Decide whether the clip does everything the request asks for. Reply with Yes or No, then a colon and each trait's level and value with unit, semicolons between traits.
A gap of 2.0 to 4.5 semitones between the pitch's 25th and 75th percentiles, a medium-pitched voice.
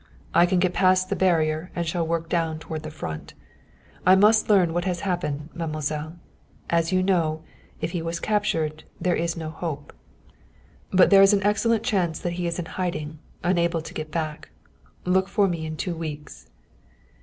Yes: average, 2.8 semitones; medium, 170 Hz